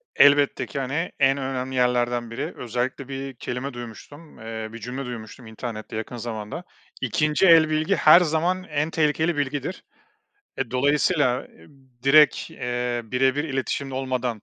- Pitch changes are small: No, average, 3.4 semitones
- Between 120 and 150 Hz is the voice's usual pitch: Yes, low, 135 Hz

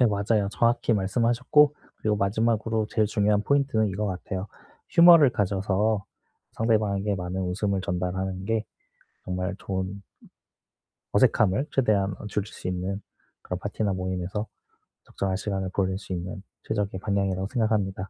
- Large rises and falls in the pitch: No, narrow, 2.5 semitones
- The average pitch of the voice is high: No, low, 100 Hz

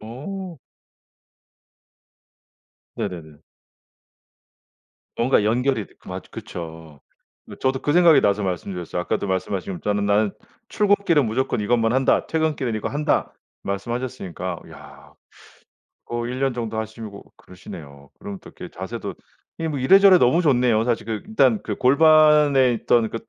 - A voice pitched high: No, low, 120 Hz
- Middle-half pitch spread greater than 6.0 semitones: No, wide, 5.6 semitones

